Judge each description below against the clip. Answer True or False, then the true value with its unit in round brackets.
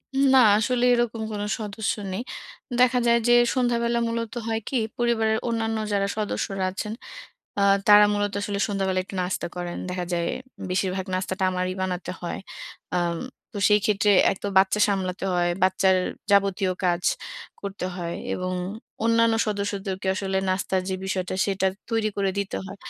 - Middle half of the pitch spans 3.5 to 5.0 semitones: False (3.0 semitones)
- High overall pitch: True (200 Hz)